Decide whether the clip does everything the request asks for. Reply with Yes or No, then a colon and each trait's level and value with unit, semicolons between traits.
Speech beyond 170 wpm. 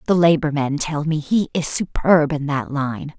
Yes: fast, 205 wpm